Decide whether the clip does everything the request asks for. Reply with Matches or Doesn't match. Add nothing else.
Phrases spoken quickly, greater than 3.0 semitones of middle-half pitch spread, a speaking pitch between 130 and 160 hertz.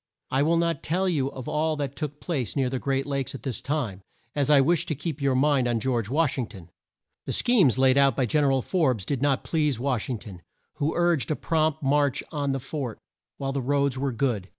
Doesn't match